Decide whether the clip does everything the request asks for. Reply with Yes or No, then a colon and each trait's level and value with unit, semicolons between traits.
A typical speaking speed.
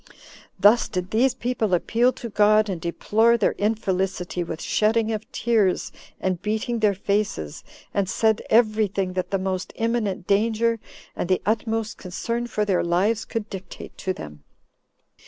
Yes: average, 155 wpm